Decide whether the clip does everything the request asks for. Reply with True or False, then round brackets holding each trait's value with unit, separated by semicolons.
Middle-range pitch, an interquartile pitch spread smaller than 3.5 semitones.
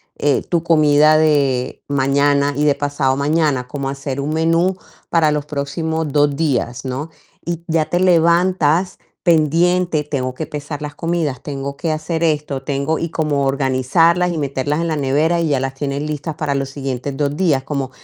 True (150 Hz; 2.7 semitones)